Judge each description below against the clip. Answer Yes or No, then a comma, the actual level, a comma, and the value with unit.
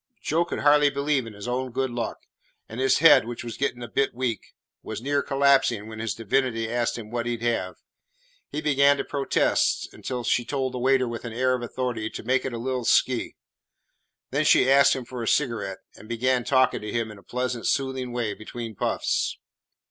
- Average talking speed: No, fast, 210 wpm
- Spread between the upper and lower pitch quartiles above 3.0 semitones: No, narrow, 2.4 semitones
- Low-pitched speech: Yes, low, 125 Hz